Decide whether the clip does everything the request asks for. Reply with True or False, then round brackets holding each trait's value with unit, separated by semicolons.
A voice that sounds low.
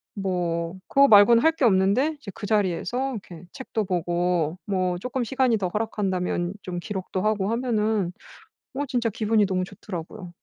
False (200 Hz)